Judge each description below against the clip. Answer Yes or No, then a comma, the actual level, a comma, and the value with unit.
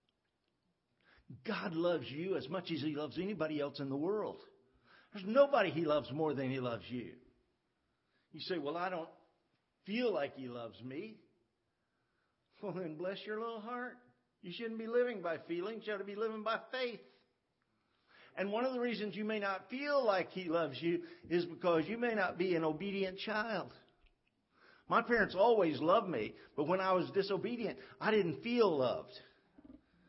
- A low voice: No, high, 190 Hz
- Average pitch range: No, wide, 5.7 semitones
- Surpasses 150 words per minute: Yes, average, 175 wpm